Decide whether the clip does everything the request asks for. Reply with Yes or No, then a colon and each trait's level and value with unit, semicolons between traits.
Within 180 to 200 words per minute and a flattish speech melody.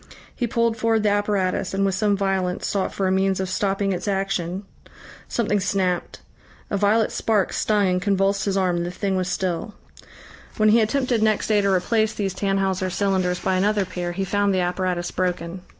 Yes: average, 190 wpm; narrow, 1.9 semitones